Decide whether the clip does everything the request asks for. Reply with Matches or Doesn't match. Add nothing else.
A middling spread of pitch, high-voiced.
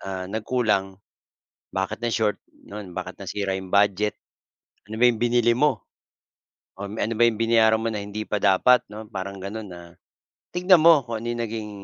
Doesn't match